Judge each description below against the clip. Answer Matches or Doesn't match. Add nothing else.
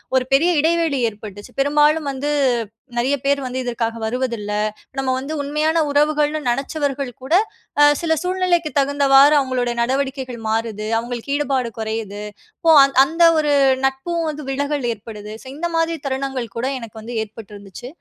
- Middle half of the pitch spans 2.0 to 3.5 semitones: Doesn't match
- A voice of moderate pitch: Doesn't match